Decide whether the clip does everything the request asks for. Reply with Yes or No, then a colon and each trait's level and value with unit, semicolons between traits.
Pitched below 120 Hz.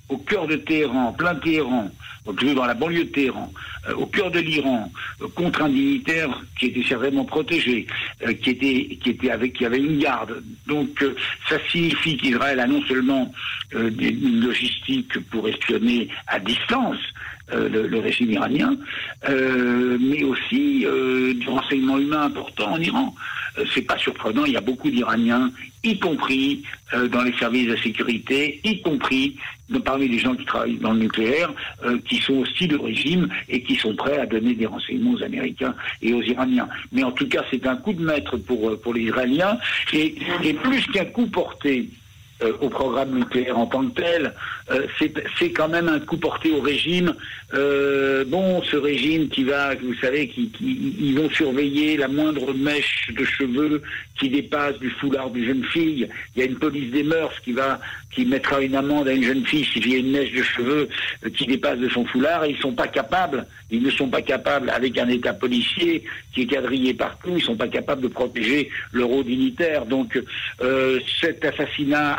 No: medium, 140 Hz